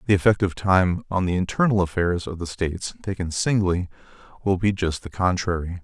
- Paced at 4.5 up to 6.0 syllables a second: Yes, 5.4 syllables/s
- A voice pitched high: No, very low, 90 Hz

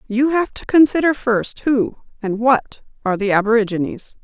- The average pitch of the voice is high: Yes, high, 240 Hz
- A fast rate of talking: No, average, 155 wpm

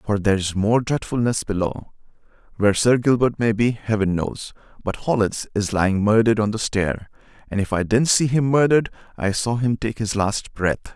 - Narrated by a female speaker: No, male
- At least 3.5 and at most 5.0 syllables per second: No, 5.2 syllables/s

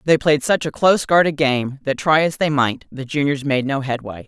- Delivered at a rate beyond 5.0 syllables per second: Yes, 5.2 syllables/s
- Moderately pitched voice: Yes, medium, 145 Hz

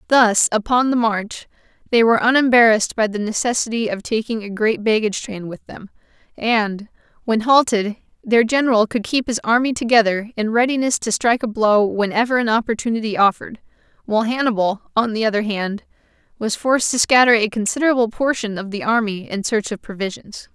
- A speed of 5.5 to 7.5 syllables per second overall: Yes, 5.7 syllables/s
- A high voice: Yes, high, 225 Hz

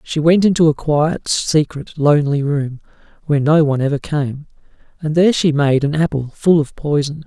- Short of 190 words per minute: Yes, average, 180 wpm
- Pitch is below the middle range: No, medium, 150 Hz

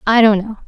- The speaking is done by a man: No, female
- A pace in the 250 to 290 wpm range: Yes, fast, 270 wpm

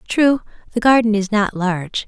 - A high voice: Yes, high, 215 Hz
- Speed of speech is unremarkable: Yes, average, 175 wpm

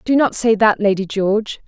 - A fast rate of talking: Yes, fast, 215 wpm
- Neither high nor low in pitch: No, high, 210 Hz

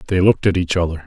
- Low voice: Yes, very low, 90 Hz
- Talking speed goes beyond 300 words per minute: No, fast, 280 wpm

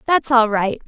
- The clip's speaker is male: No, female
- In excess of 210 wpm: No, fast, 205 wpm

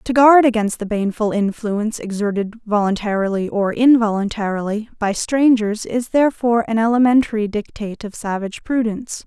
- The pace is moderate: No, slow, 130 wpm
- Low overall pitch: No, high, 220 Hz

